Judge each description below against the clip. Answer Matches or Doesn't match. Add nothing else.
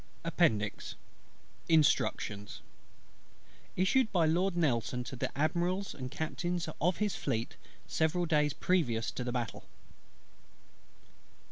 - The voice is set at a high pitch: Doesn't match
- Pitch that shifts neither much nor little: Doesn't match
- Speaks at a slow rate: Matches